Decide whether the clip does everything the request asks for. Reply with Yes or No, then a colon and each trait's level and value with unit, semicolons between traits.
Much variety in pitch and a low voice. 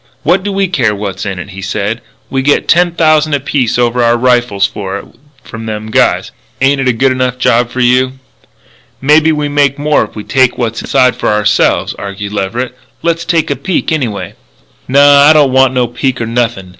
No: average, 4.4 semitones; low, 125 Hz